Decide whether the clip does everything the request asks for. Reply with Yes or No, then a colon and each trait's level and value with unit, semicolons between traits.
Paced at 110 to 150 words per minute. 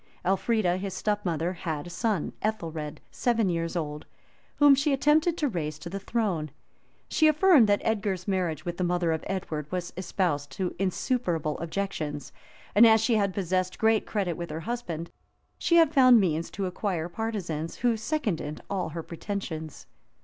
No: average, 165 wpm